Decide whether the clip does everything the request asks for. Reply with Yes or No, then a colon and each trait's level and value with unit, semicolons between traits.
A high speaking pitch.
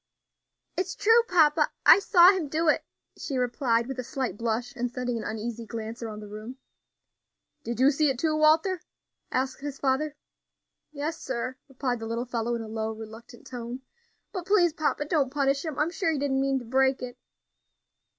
Yes: very high, 265 Hz